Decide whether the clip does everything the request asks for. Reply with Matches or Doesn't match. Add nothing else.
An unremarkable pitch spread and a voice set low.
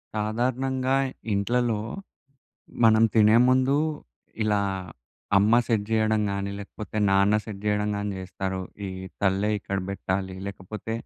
Doesn't match